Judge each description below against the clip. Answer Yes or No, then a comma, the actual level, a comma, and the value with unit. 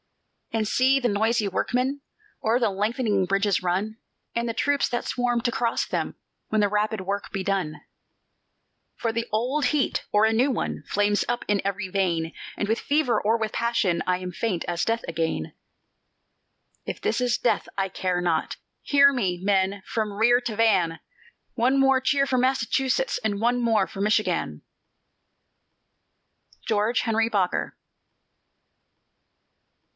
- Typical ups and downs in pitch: Yes, average, 3.7 semitones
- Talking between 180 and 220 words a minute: No, average, 150 wpm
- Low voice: No, high, 220 Hz